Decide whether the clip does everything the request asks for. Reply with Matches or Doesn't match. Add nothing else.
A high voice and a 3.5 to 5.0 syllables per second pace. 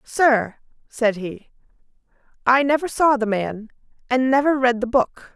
Matches